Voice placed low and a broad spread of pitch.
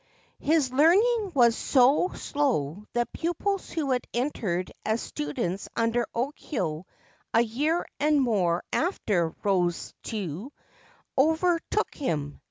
No: high, 245 Hz; wide, 8.3 semitones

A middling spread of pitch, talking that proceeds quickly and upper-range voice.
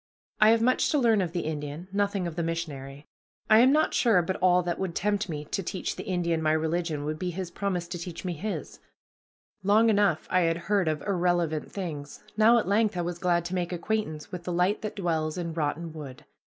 No: average, 3.7 semitones; fast, 220 wpm; medium, 175 Hz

